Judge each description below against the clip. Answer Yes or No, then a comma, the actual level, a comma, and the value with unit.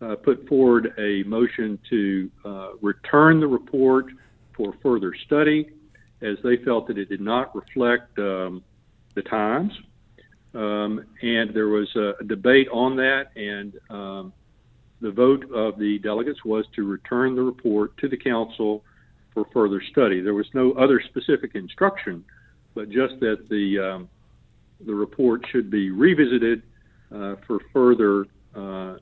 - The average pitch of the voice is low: Yes, low, 110 Hz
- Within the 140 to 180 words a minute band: Yes, average, 145 wpm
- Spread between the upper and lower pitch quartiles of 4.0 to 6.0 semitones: No, average, 3.4 semitones